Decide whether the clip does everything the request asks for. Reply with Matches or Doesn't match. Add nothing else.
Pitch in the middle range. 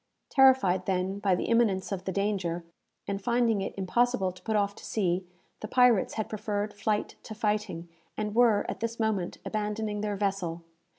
Doesn't match